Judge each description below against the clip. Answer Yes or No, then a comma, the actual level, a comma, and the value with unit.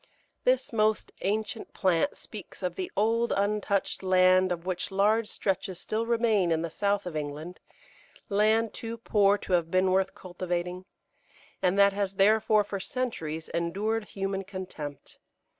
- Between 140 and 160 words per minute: Yes, average, 145 wpm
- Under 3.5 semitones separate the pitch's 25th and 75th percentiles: Yes, average, 2.9 semitones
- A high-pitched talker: Yes, high, 195 Hz